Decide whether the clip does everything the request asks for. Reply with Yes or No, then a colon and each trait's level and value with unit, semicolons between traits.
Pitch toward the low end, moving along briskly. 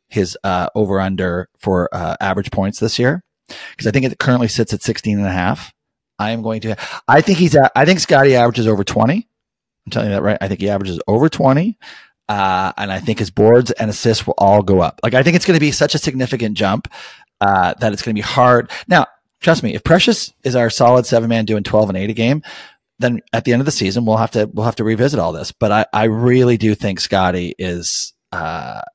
Yes: low, 115 Hz; fast, 245 wpm